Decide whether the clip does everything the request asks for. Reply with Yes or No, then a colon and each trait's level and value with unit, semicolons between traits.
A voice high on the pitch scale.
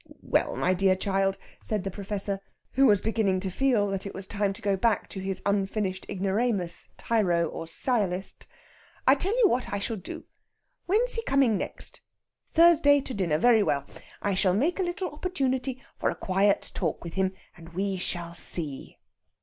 Yes: high, 200 Hz